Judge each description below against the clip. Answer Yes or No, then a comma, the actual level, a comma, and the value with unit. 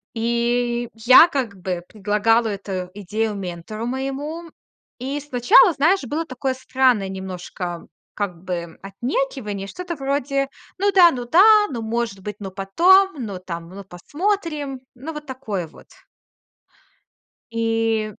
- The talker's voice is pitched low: No, high, 235 Hz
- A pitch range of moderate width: No, wide, 6.1 semitones